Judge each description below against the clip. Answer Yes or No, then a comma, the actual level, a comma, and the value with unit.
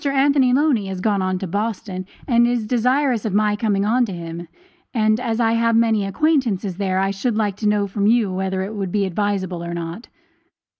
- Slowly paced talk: No, fast, 205 wpm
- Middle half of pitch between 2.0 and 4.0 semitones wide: Yes, average, 3.4 semitones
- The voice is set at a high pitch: Yes, high, 210 Hz